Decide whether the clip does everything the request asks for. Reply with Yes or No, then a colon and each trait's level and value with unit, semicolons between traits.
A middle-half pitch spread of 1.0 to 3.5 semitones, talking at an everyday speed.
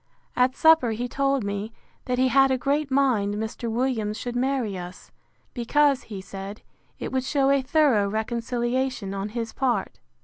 No: average, 3.9 semitones; average, 165 wpm